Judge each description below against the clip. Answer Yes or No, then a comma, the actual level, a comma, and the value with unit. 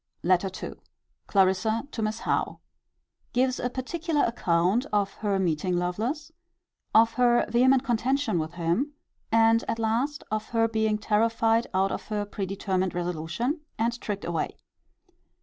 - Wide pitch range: No, average, 4.1 semitones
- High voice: Yes, high, 220 Hz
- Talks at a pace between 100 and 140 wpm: Yes, slow, 135 wpm